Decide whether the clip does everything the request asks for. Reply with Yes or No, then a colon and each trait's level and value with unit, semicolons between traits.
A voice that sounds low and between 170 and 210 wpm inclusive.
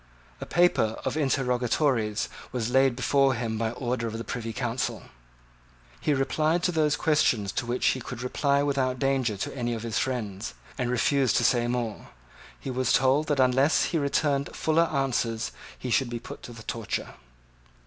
Yes: low, 125 Hz; average, 175 wpm